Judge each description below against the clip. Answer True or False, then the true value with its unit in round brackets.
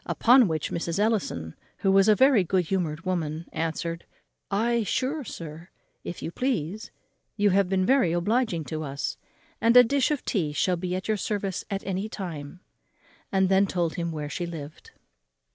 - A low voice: False (185 Hz)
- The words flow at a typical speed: True (175 wpm)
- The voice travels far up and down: False (4.5 semitones)